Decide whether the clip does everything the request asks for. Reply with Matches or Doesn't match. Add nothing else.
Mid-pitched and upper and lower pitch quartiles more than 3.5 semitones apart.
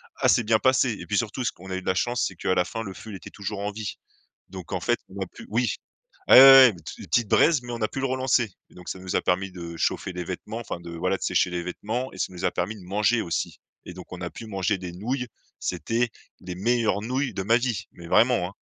Doesn't match